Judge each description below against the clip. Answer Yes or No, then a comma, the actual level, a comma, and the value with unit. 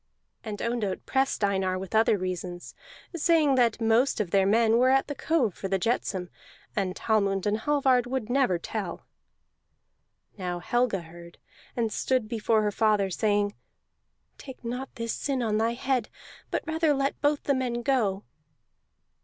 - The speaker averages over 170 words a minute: No, average, 155 wpm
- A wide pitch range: No, average, 4.8 semitones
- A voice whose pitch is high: Yes, high, 225 Hz